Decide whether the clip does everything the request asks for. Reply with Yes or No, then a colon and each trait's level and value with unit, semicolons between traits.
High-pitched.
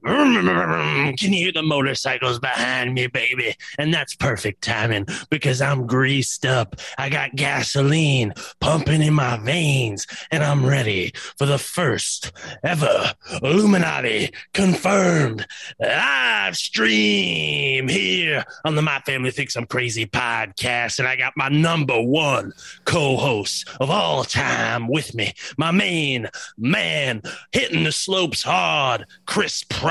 No: low, 135 Hz